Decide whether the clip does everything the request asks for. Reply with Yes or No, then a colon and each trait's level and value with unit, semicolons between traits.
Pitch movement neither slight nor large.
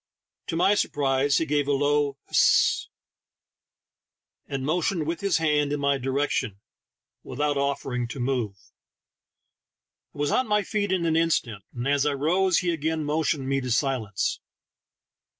Yes: average, 3.3 semitones